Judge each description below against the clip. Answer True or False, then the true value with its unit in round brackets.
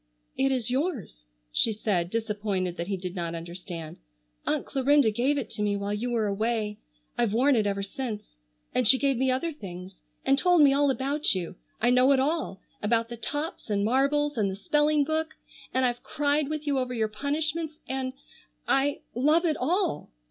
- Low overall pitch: False (250 Hz)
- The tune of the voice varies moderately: False (5.8 semitones)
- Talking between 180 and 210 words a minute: True (185 wpm)